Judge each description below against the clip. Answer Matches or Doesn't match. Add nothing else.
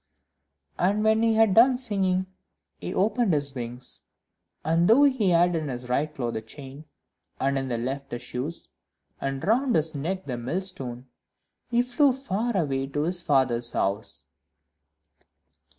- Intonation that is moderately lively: Doesn't match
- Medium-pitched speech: Matches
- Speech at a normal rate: Matches